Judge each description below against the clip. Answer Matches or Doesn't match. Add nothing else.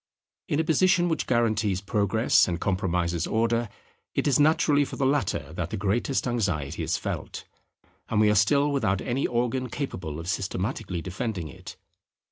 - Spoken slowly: Doesn't match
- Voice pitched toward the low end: Matches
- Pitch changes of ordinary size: Doesn't match